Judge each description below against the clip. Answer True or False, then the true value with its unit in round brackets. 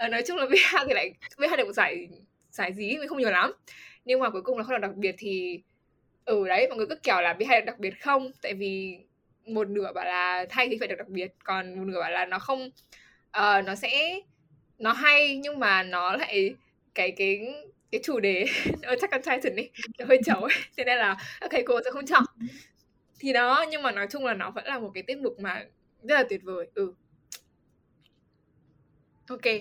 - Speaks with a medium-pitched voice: False (225 Hz)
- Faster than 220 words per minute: True (230 wpm)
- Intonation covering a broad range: True (6.2 semitones)